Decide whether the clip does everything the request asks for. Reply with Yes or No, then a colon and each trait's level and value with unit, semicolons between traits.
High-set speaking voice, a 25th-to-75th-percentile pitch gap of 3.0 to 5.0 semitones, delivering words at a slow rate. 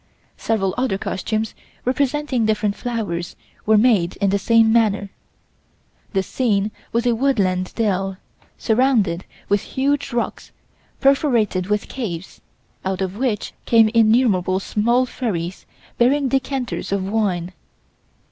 Yes: high, 220 Hz; average, 4.2 semitones; slow, 120 wpm